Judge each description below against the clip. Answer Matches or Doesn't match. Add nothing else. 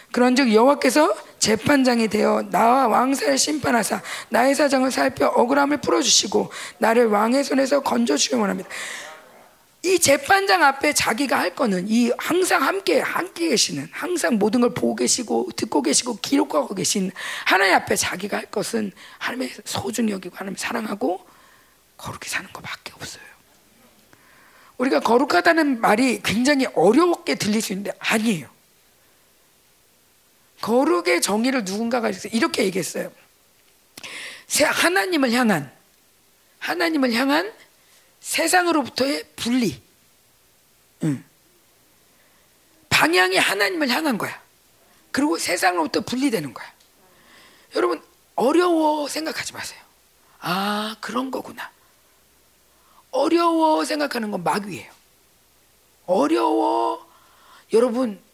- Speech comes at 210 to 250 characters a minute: Doesn't match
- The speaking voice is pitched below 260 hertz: Doesn't match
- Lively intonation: Matches